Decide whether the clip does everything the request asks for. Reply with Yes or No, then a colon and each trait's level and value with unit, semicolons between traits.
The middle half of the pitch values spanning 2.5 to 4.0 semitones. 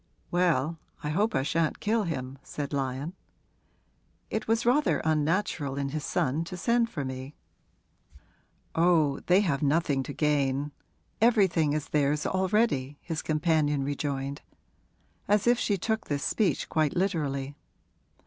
No: average, 5.0 semitones